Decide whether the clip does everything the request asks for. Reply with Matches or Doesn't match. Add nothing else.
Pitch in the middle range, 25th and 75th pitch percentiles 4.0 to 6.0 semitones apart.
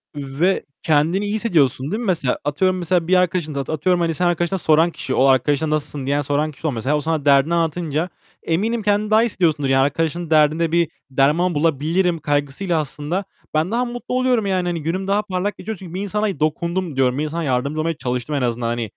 Matches